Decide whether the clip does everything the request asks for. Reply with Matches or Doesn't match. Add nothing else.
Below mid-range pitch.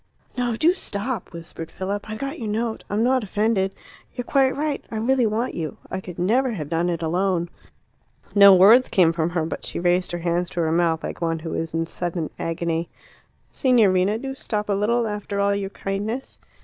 Doesn't match